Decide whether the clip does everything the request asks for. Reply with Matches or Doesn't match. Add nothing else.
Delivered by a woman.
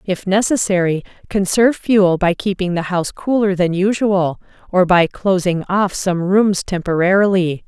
Matches